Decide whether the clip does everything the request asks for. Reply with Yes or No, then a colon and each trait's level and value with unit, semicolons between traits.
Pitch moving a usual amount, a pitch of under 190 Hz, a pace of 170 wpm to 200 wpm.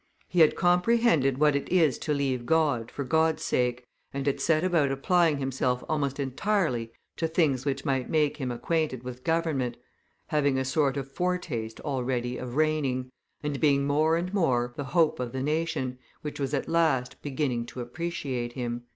Yes: average, 3.9 semitones; medium, 140 Hz; average, 175 wpm